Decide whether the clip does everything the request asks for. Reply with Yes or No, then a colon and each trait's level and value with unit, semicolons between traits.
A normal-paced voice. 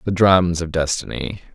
Yes: average, 155 wpm